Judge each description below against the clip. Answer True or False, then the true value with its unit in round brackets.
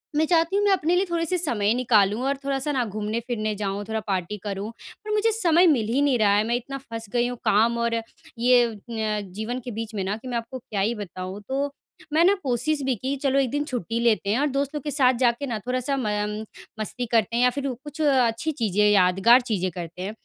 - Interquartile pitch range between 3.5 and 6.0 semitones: True (4.7 semitones)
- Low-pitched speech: False (240 Hz)